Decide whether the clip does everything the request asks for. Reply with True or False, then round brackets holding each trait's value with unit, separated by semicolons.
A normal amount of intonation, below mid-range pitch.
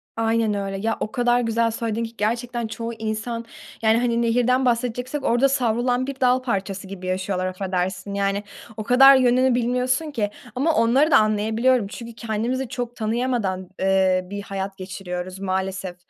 False (3.9 semitones; 225 Hz)